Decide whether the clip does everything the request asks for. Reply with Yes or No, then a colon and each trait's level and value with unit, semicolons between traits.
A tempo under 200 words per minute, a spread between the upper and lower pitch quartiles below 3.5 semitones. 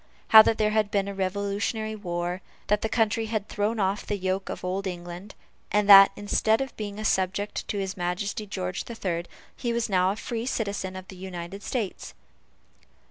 Yes: average, 190 wpm; narrow, 2.4 semitones